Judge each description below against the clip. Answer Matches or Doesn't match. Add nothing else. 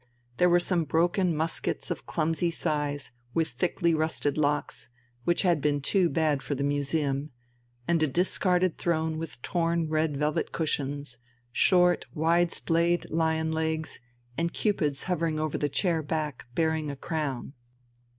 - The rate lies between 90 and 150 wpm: Matches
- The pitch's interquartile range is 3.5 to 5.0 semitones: Doesn't match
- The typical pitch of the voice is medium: Matches